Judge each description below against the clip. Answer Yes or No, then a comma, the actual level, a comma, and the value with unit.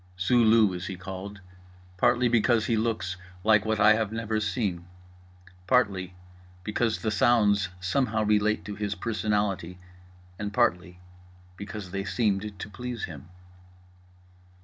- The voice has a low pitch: Yes, low, 105 Hz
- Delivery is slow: Yes, slow, 125 wpm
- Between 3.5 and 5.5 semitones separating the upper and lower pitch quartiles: No, average, 2.7 semitones